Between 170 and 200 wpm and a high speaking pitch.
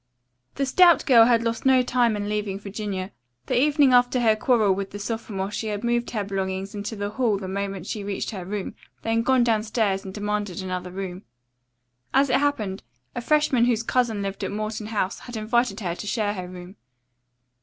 Yes: average, 195 wpm; high, 210 Hz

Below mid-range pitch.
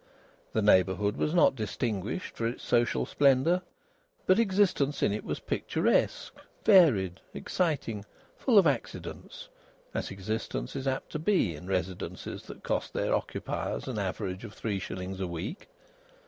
Yes: low, 115 Hz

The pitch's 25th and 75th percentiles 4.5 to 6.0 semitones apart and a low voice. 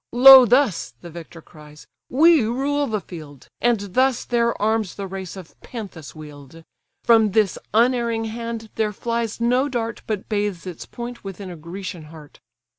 No: average, 5.3 semitones; high, 215 Hz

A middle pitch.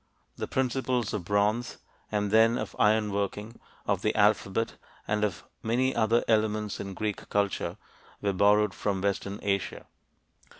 No: low, 105 Hz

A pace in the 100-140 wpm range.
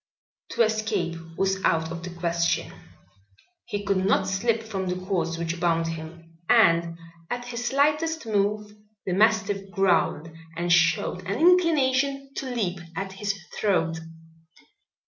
Yes: slow, 135 wpm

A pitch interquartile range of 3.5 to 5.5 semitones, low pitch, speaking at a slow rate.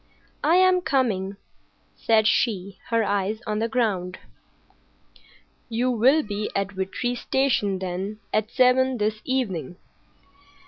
No: average, 4.3 semitones; high, 215 Hz; slow, 120 wpm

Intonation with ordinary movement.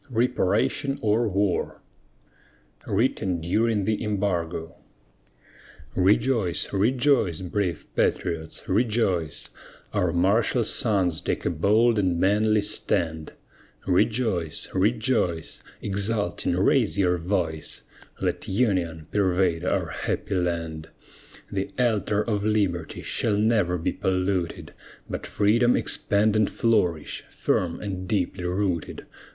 Yes: average, 3.7 semitones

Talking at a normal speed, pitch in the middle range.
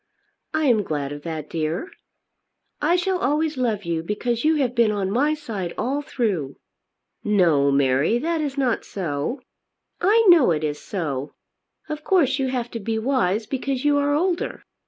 No: average, 170 wpm; high, 235 Hz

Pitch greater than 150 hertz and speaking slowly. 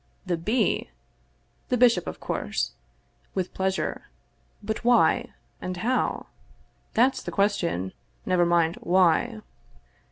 Yes: high, 190 Hz; slow, 105 wpm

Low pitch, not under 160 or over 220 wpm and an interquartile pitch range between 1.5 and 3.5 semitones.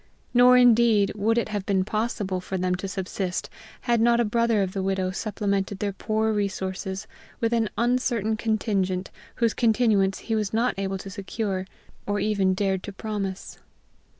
No: high, 205 Hz; average, 165 wpm; average, 2.9 semitones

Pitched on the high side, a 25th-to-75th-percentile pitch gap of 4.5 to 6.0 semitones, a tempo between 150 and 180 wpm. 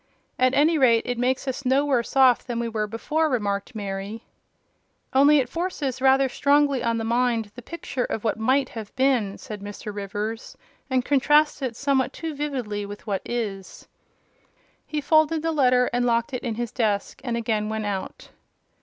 No: high, 245 Hz; average, 3.9 semitones; average, 175 wpm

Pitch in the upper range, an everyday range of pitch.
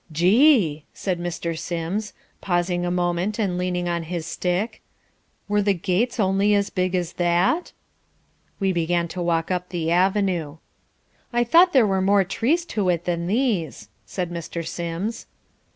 No: medium, 180 Hz; average, 3.0 semitones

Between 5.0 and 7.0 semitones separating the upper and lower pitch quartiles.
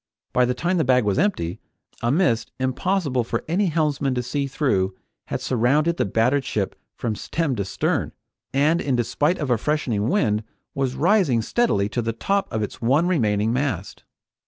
Yes: wide, 5.4 semitones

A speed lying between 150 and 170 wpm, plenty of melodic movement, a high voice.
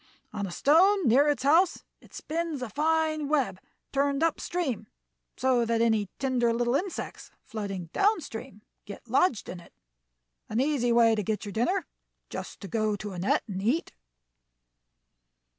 Yes: average, 160 wpm; wide, 6.1 semitones; high, 245 Hz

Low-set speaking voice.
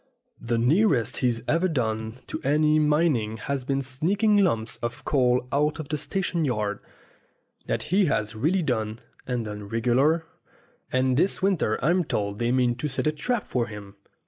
Yes: low, 130 Hz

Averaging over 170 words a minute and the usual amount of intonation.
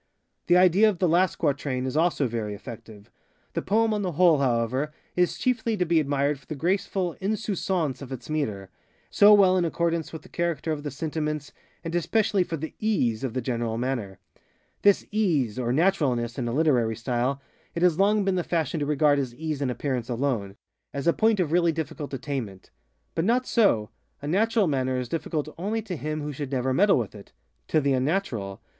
No: average, 190 wpm; wide, 5.9 semitones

